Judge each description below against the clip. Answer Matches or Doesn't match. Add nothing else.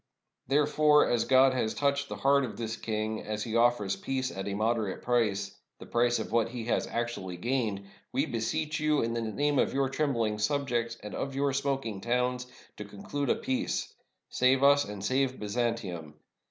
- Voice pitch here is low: Matches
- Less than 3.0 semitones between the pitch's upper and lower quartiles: Doesn't match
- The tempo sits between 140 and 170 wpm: Doesn't match